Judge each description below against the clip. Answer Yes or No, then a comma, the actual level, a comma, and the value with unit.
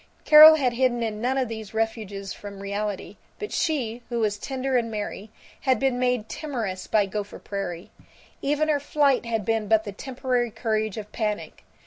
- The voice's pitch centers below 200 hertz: No, high, 225 Hz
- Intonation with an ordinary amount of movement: Yes, average, 3.8 semitones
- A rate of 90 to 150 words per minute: No, average, 175 wpm